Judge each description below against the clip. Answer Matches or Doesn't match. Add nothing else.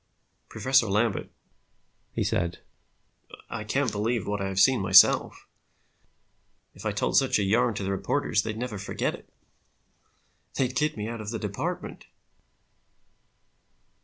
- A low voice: Matches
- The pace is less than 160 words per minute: Matches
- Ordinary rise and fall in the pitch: Matches